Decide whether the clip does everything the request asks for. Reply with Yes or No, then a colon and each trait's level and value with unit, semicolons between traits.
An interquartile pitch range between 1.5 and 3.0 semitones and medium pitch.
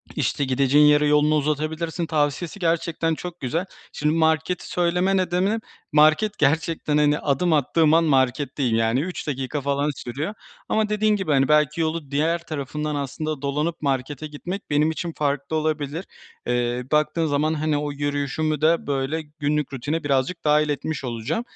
Yes: narrow, 2.5 semitones; medium, 150 Hz